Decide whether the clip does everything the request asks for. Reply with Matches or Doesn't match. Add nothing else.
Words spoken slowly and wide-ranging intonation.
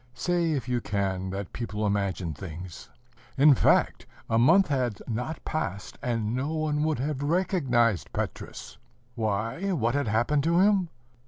Doesn't match